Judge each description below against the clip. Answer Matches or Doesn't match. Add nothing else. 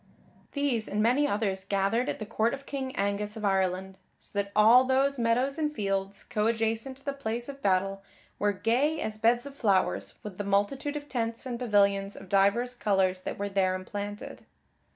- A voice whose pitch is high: Matches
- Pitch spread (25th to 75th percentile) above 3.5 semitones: Matches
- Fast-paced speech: Doesn't match